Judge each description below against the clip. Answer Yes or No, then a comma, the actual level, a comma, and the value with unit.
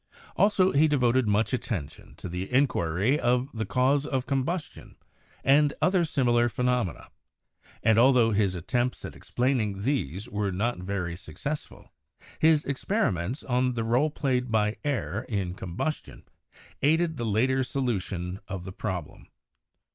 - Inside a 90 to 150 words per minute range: Yes, slow, 135 wpm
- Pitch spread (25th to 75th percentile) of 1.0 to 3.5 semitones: No, wide, 5.6 semitones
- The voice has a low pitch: Yes, low, 120 Hz